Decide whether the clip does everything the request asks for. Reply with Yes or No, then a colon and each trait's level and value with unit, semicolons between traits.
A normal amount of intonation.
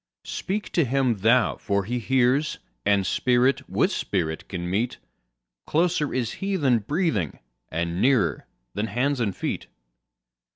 No: wide, 6.0 semitones